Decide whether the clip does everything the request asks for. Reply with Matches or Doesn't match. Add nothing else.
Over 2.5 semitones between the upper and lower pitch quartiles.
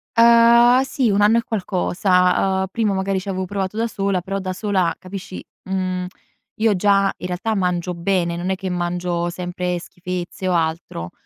Doesn't match